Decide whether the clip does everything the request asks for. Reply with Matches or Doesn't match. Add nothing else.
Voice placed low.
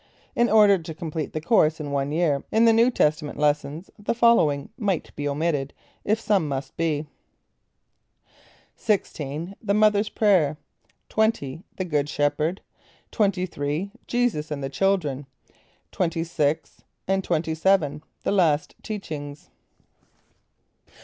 Doesn't match